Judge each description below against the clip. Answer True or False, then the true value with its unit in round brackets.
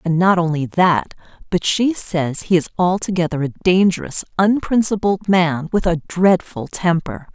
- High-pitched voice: False (180 Hz)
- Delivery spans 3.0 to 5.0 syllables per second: True (4.5 syllables/s)